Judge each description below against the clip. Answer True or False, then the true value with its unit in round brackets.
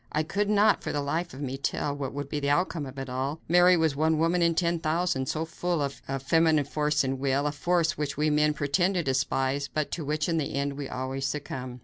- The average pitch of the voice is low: False (150 Hz)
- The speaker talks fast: True (255 wpm)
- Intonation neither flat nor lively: True (3.0 semitones)